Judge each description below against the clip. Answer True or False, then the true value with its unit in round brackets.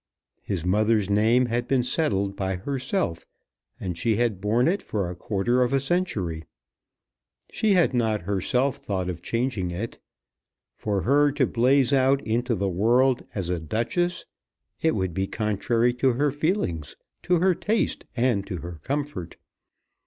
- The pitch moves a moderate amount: False (5.8 semitones)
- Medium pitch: False (115 Hz)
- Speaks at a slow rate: False (155 wpm)